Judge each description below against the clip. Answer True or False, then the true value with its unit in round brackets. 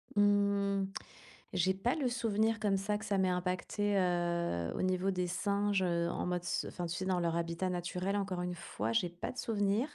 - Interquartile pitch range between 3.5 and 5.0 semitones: False (2.5 semitones)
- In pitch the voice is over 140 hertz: True (190 Hz)